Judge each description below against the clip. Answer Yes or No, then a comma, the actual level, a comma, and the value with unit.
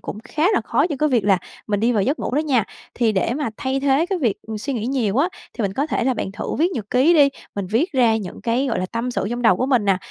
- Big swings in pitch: No, average, 4.7 semitones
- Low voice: No, high, 245 Hz